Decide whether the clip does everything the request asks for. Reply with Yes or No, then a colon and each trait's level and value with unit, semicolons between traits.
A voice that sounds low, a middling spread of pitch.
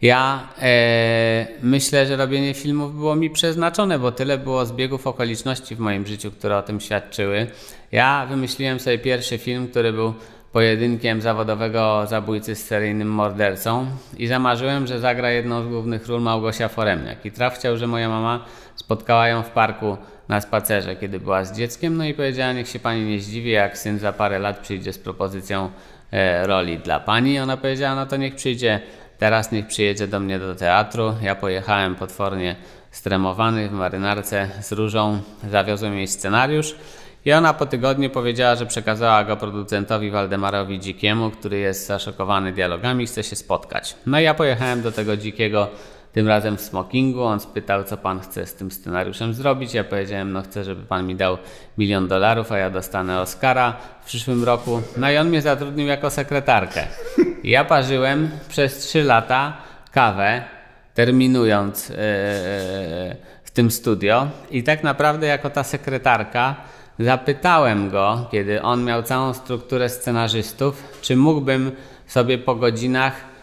Yes: low, 115 Hz; average, 4.2 semitones